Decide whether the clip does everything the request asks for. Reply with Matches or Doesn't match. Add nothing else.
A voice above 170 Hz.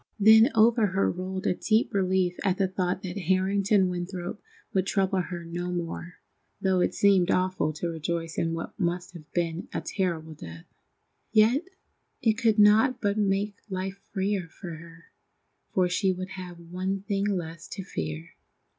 Matches